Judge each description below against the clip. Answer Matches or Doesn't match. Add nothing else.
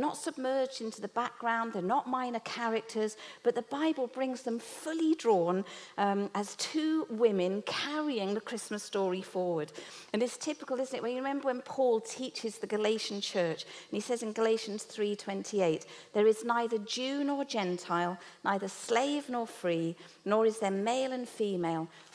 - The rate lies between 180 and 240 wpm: Doesn't match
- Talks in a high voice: Matches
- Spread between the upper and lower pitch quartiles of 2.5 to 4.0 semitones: Doesn't match